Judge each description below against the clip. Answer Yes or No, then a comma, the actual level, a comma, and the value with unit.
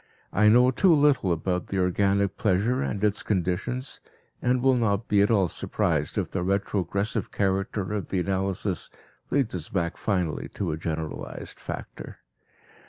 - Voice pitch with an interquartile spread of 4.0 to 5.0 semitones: No, average, 3.3 semitones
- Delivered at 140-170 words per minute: Yes, average, 150 wpm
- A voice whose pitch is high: No, low, 100 Hz